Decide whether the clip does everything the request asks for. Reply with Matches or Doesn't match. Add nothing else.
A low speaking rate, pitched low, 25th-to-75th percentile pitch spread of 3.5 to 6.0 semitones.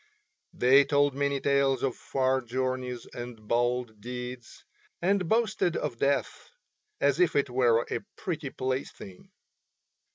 Doesn't match